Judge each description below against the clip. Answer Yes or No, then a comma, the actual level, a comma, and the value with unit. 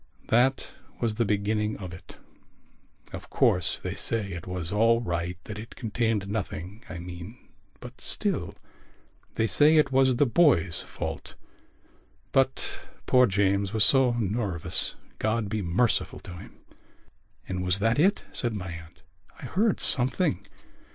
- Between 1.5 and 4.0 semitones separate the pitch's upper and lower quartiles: No, average, 4.7 semitones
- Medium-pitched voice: No, low, 105 Hz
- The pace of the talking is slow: No, average, 145 wpm